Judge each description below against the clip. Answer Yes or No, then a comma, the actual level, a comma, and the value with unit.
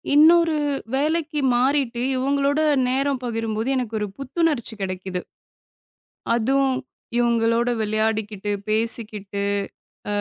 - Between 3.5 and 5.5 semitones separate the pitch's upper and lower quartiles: Yes, average, 4.2 semitones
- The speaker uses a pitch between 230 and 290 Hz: Yes, high, 240 Hz